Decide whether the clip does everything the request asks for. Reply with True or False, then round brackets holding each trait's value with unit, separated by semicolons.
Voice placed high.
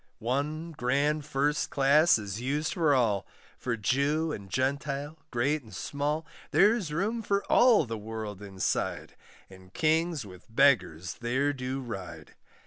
False (135 Hz)